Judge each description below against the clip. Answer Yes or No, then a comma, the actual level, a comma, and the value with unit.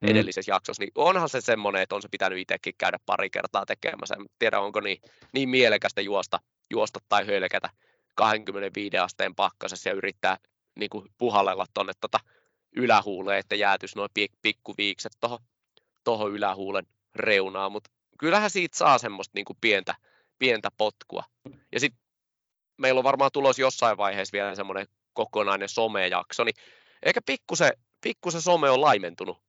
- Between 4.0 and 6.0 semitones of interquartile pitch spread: Yes, average, 5.1 semitones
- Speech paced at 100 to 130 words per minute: No, average, 150 wpm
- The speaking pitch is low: Yes, low, 110 Hz